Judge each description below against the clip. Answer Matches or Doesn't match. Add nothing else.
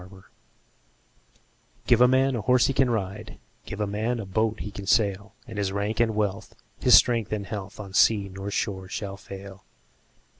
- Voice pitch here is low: Matches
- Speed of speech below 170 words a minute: Doesn't match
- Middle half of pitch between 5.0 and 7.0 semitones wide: Doesn't match